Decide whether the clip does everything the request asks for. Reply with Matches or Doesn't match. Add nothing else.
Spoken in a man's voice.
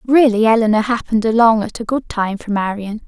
Doesn't match